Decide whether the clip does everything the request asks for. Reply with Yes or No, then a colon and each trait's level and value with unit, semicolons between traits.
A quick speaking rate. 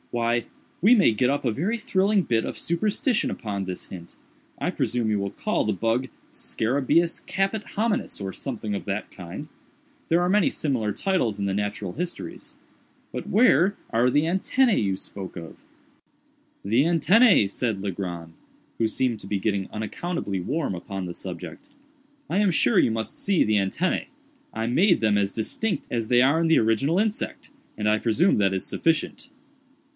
No: average, 170 wpm